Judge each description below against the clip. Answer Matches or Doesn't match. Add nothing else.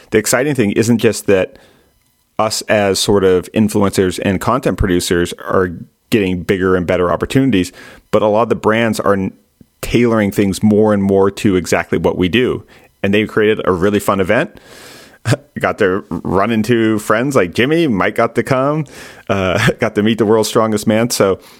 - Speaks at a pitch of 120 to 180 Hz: Doesn't match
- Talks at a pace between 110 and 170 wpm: Doesn't match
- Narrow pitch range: Doesn't match